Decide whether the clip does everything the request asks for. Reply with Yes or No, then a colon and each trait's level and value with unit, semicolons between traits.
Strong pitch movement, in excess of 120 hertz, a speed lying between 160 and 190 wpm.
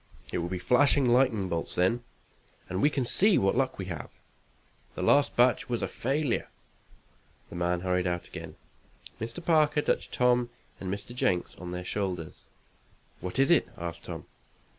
No: wide, 6.8 semitones; low, 115 Hz; average, 165 wpm